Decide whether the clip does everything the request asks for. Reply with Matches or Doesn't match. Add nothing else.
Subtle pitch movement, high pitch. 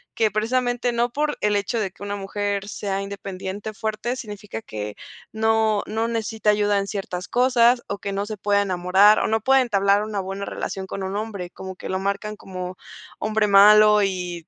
Matches